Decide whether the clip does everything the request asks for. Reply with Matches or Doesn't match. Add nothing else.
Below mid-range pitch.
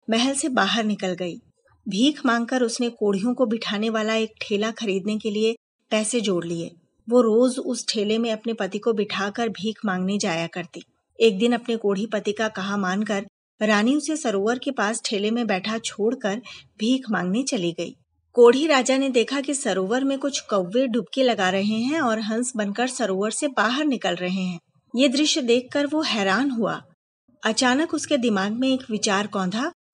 Doesn't match